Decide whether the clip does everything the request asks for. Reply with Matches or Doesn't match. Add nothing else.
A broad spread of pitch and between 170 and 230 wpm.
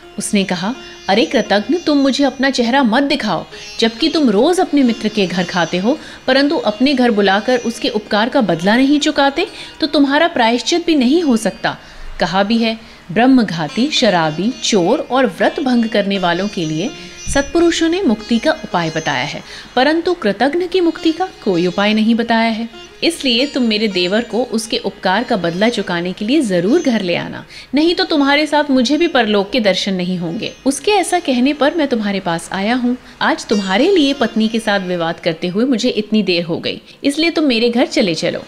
Matches